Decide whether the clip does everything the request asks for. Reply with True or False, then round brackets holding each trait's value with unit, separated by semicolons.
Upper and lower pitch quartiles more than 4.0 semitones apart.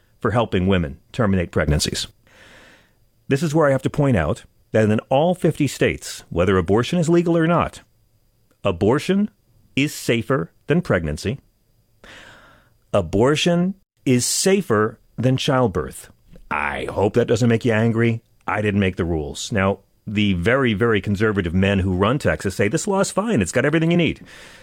True (5.2 semitones)